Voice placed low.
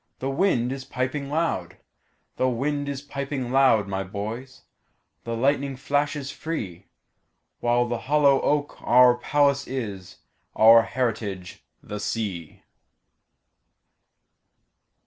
Yes: low, 130 Hz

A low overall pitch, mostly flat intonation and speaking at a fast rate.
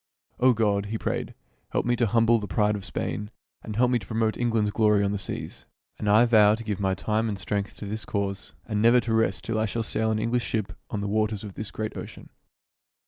Yes: low, 110 Hz; narrow, 1.8 semitones; fast, 240 wpm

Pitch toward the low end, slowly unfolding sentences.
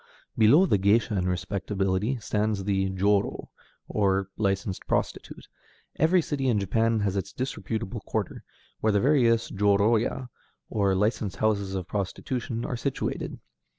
Yes: low, 105 Hz; slow, 130 wpm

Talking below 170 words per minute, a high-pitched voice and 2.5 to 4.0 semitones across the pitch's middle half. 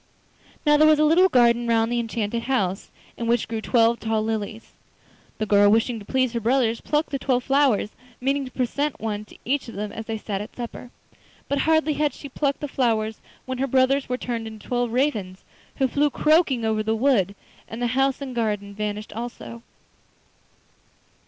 No: average, 190 wpm; high, 235 Hz; average, 3.7 semitones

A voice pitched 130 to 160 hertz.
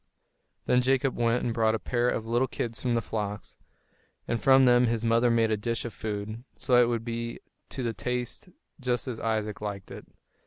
No: low, 115 Hz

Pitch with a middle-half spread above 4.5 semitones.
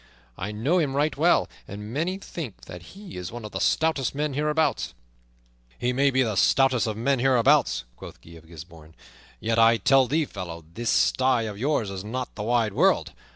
Yes: average, 5.3 semitones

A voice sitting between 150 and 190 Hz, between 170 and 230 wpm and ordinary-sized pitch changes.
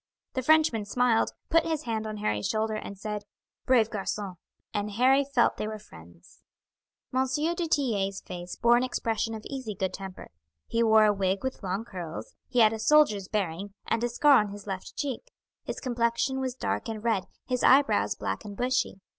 No: high, 220 Hz; average, 190 wpm; average, 4.3 semitones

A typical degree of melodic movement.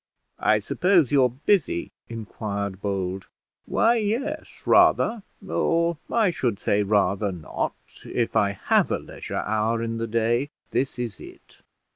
No: wide, 7.9 semitones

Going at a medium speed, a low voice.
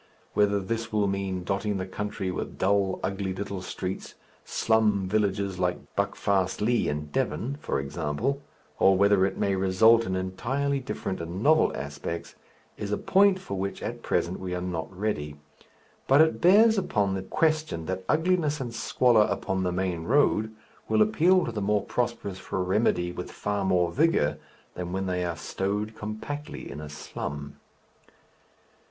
Yes: average, 160 wpm; low, 100 Hz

